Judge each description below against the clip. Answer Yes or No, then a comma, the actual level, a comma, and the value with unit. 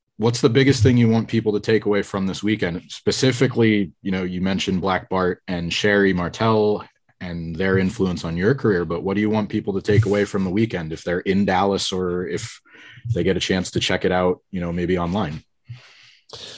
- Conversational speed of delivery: No, fast, 215 wpm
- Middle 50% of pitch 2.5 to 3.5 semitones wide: Yes, average, 3.0 semitones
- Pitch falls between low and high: No, low, 100 Hz